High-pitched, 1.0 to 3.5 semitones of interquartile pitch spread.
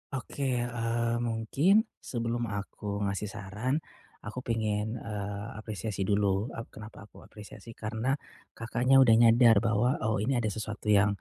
No: low, 110 Hz; narrow, 2.4 semitones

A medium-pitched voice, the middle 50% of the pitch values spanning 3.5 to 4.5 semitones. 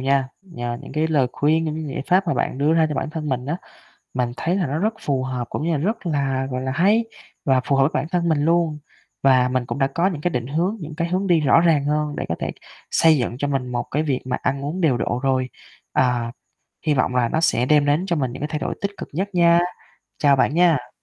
Yes: medium, 150 Hz; average, 4.1 semitones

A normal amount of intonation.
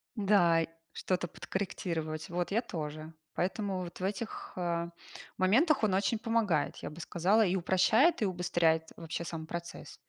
Yes: average, 3.4 semitones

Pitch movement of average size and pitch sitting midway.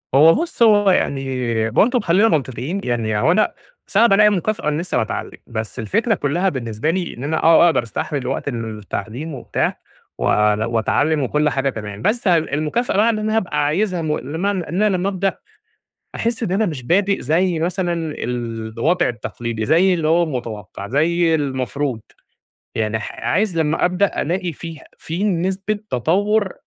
No: wide, 7.5 semitones; medium, 160 Hz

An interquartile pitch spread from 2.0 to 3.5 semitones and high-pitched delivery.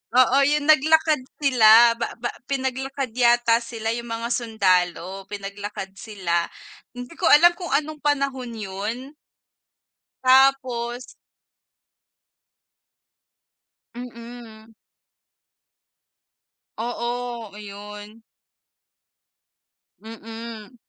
Yes: average, 3.1 semitones; high, 235 Hz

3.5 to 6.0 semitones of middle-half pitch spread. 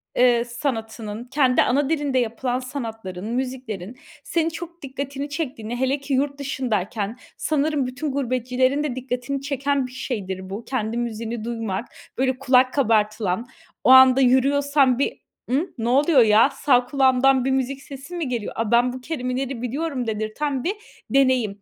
No: average, 3.0 semitones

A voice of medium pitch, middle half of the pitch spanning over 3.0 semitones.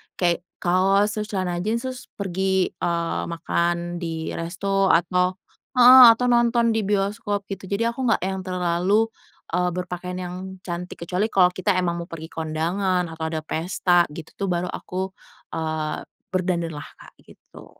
No: medium, 180 Hz; narrow, 2.6 semitones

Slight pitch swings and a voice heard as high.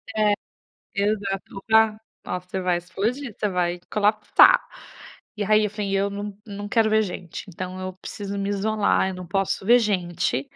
Yes: narrow, 2.3 semitones; high, 200 Hz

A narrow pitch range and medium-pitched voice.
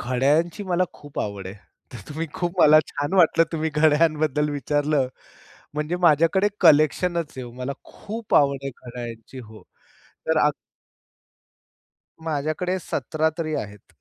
No: average, 3.3 semitones; medium, 150 Hz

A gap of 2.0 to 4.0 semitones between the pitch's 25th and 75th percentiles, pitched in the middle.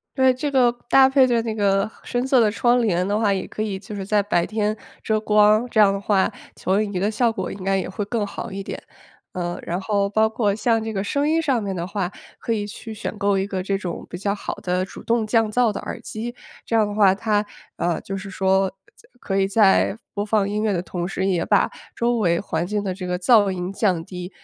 No: narrow, 2.5 semitones; high, 205 Hz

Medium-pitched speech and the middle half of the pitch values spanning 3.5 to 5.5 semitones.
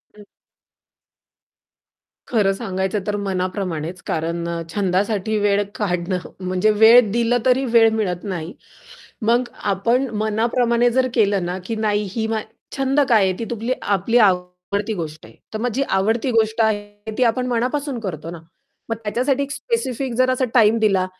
No: high, 215 Hz; average, 4.0 semitones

